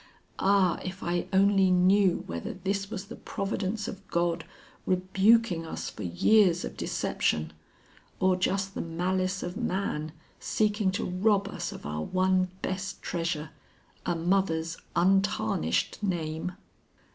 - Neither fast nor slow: No, slow, 130 wpm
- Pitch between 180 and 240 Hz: Yes, medium, 185 Hz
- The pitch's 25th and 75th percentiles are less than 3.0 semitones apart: Yes, narrow, 2.6 semitones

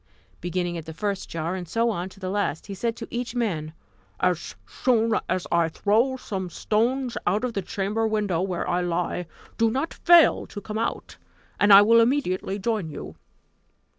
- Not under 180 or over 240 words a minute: Yes, average, 185 wpm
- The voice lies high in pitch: Yes, high, 205 Hz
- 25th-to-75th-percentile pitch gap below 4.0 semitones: No, average, 4.4 semitones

